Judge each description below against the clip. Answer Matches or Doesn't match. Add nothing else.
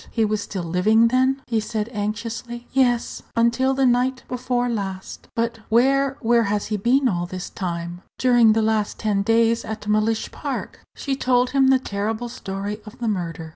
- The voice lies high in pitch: Matches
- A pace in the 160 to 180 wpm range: Matches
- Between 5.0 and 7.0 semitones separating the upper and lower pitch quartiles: Doesn't match